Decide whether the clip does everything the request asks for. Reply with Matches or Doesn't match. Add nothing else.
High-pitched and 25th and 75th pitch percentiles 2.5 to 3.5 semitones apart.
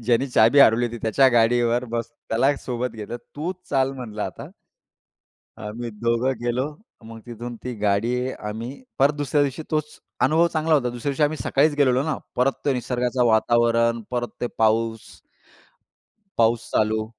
Doesn't match